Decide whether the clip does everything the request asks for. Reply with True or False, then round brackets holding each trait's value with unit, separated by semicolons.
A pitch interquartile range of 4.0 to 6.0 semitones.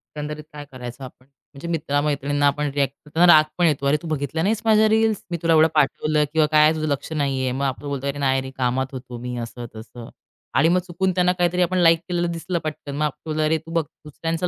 False (3.3 semitones)